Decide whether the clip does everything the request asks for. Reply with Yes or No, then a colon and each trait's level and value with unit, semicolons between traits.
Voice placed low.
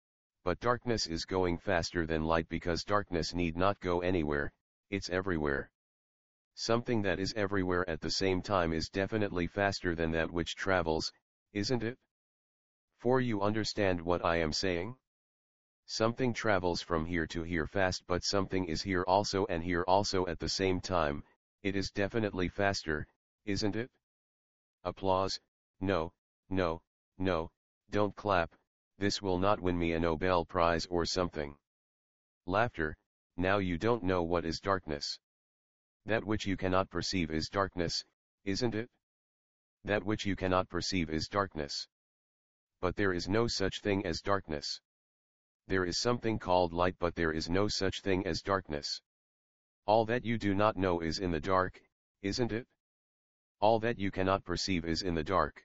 Yes: very low, 95 Hz